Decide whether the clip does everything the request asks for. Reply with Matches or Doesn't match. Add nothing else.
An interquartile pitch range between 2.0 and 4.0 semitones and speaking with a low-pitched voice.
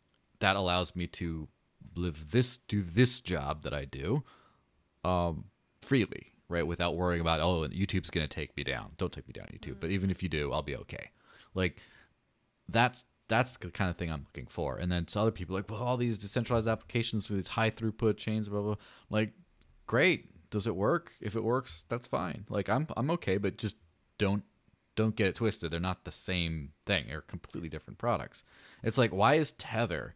Doesn't match